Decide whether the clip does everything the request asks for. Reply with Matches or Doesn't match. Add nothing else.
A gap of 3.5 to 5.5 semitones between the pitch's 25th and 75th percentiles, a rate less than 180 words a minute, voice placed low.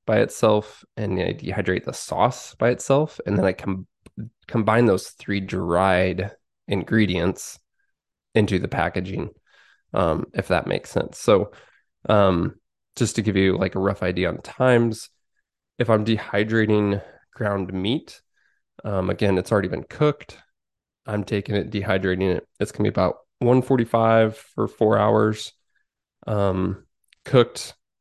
Doesn't match